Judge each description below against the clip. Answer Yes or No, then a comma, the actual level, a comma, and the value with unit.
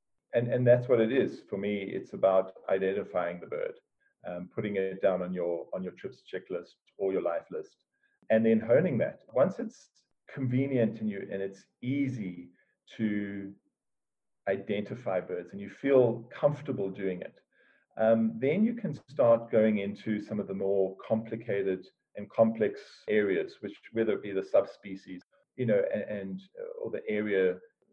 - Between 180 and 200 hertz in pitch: No, low, 110 Hz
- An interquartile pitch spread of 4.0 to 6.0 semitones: Yes, average, 4.6 semitones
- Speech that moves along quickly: No, average, 165 wpm